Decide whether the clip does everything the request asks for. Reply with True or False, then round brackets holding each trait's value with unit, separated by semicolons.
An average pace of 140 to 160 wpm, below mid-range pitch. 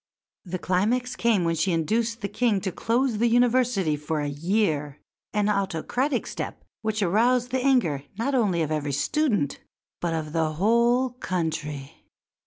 False (155 wpm; 200 Hz)